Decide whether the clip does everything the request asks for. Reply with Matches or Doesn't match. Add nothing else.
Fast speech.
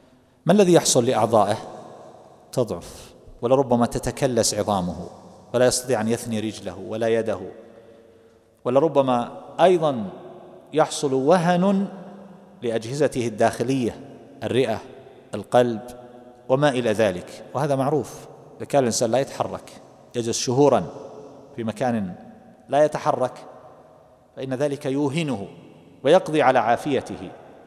Doesn't match